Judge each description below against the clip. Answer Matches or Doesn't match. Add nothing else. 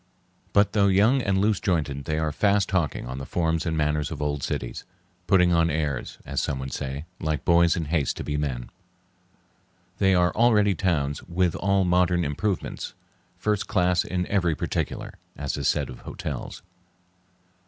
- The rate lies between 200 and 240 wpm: Doesn't match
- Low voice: Matches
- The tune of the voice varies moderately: Matches